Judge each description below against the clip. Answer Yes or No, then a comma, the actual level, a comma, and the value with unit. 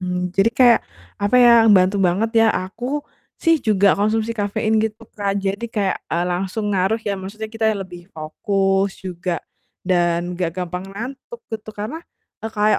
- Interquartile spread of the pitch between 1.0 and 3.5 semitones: Yes, average, 3.1 semitones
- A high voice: Yes, high, 200 Hz